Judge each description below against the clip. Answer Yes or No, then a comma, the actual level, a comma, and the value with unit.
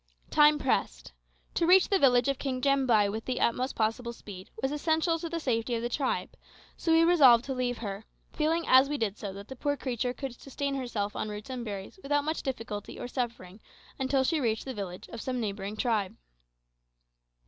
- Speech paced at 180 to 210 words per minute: Yes, average, 200 wpm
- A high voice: Yes, very high, 250 Hz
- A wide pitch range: No, average, 4.5 semitones